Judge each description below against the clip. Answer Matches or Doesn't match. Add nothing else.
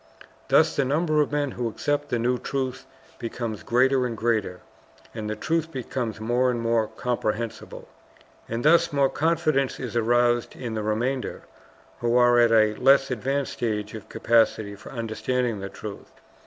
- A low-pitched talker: Matches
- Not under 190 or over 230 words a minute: Doesn't match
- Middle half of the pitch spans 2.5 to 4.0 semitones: Matches